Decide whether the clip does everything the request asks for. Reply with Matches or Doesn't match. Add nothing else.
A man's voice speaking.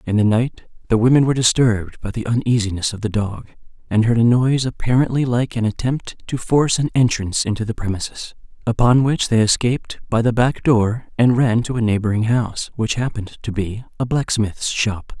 Matches